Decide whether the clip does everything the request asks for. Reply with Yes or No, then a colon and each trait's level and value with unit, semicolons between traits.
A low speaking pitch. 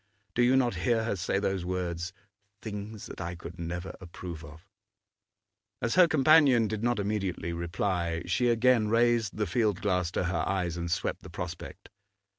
Yes: low, 100 Hz